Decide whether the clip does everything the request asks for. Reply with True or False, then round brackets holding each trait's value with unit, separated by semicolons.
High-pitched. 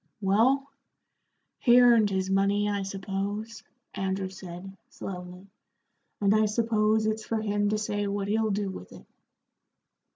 True (205 Hz)